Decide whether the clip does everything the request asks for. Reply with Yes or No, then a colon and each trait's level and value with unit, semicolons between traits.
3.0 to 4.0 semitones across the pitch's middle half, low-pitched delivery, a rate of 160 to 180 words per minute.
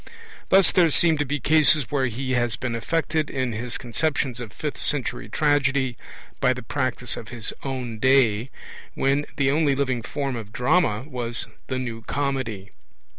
Yes: average, 3.3 semitones; low, 130 Hz; average, 165 wpm